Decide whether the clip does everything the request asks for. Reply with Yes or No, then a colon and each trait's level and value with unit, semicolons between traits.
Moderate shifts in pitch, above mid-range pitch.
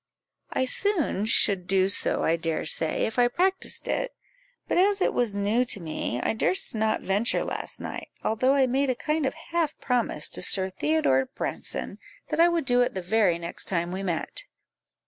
No: wide, 7.1 semitones; high, 225 Hz